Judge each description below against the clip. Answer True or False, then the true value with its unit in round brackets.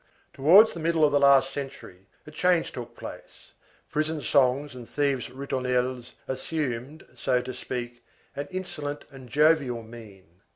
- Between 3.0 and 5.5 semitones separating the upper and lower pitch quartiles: True (3.3 semitones)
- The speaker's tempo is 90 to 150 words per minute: True (140 wpm)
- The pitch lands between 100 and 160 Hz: True (135 Hz)